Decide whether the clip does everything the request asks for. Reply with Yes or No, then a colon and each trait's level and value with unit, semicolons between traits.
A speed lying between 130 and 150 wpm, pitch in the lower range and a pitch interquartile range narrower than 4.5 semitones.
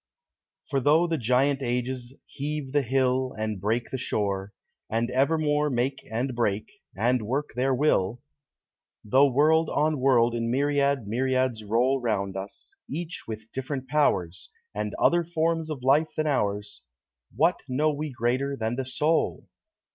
Yes: average, 145 wpm; low, 130 Hz; average, 3.9 semitones